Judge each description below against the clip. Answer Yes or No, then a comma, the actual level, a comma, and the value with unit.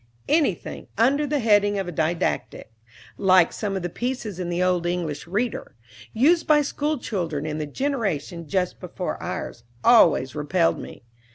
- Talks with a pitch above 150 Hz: Yes, medium, 185 Hz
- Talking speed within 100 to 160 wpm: Yes, average, 155 wpm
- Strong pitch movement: Yes, wide, 6.5 semitones